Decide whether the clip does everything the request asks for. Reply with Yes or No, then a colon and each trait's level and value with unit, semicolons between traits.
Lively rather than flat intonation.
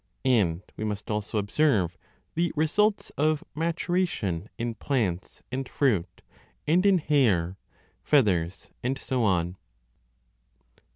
Yes: wide, 8.1 semitones